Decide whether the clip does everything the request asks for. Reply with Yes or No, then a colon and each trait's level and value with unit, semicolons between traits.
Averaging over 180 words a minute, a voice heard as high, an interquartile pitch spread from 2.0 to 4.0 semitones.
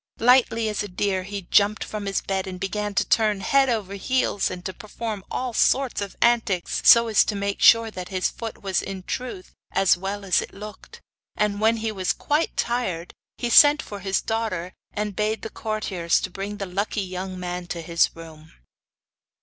Yes: average, 190 wpm; high, 200 Hz; average, 3.1 semitones